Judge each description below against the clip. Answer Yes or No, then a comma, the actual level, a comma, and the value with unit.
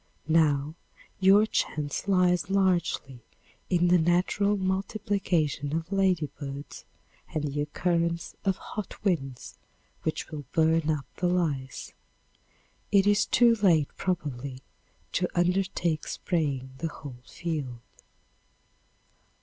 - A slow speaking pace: Yes, slow, 105 wpm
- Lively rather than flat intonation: No, average, 4.3 semitones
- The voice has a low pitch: No, medium, 170 Hz